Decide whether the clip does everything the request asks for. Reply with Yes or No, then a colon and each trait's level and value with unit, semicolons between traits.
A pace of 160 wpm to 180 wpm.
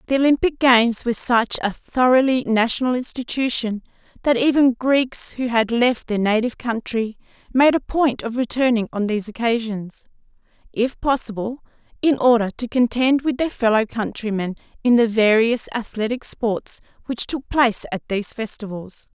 No: average, 145 wpm